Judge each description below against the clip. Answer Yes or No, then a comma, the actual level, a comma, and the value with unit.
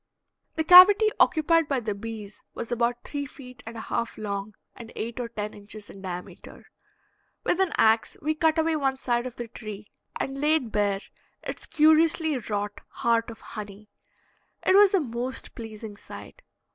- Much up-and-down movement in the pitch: Yes, wide, 6.4 semitones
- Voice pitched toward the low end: No, high, 235 Hz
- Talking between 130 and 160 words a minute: No, average, 170 wpm